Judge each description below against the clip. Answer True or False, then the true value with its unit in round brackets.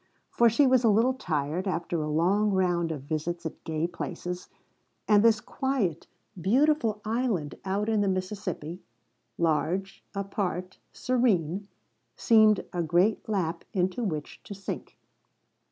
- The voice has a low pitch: False (190 Hz)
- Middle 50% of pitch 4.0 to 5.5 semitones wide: True (4.3 semitones)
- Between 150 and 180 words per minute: False (135 wpm)